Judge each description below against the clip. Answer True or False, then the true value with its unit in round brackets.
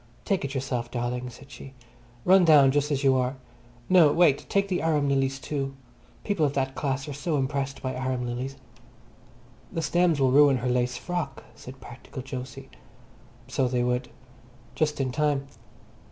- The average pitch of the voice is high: False (135 Hz)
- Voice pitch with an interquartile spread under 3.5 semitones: True (2.5 semitones)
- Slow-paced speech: False (170 wpm)